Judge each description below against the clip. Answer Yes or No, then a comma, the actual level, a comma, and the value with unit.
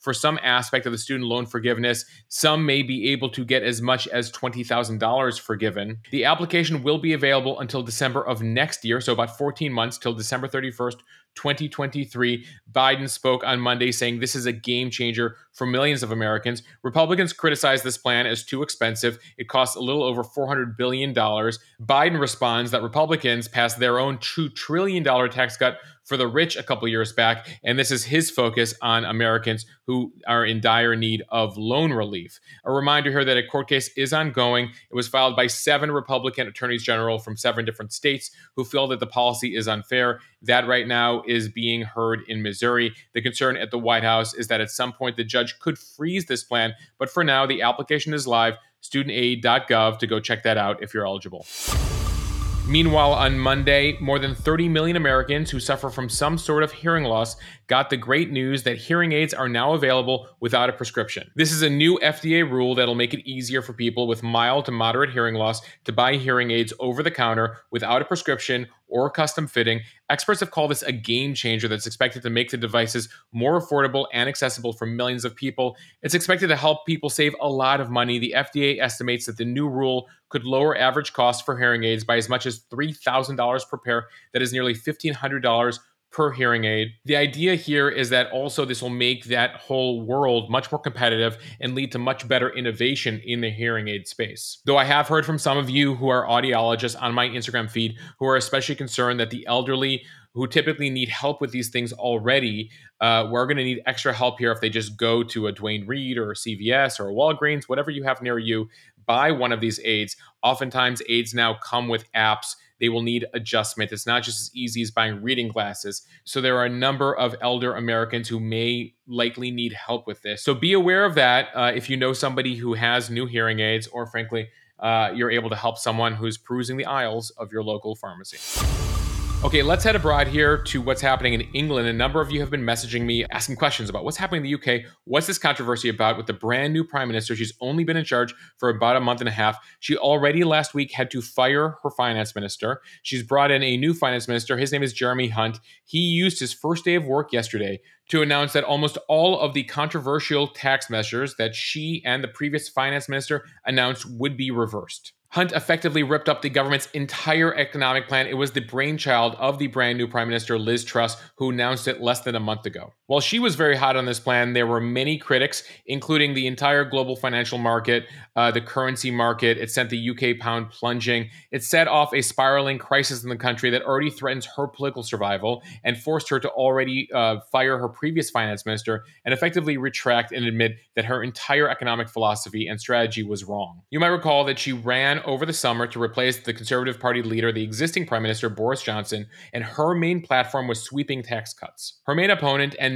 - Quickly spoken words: Yes, fast, 210 wpm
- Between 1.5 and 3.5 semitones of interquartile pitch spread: Yes, average, 3.2 semitones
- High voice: No, low, 125 Hz